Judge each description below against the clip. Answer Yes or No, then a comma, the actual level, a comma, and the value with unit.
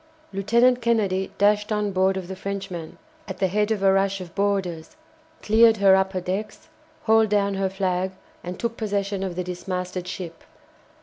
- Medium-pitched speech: No, high, 195 Hz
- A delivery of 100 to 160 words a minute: No, average, 170 wpm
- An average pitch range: No, narrow, 2.0 semitones